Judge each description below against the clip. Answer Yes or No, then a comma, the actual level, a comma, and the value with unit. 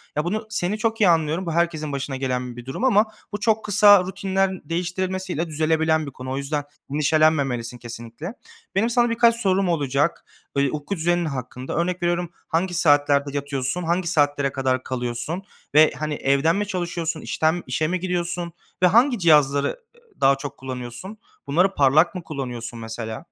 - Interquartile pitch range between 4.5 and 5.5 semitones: Yes, average, 5.1 semitones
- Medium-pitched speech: Yes, medium, 160 Hz